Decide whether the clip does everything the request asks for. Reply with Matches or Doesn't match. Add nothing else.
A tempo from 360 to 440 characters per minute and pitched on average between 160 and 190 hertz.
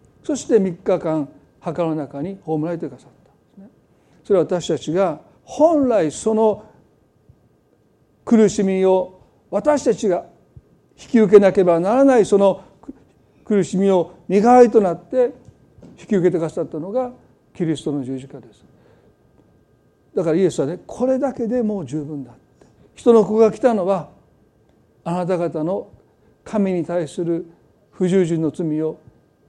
Doesn't match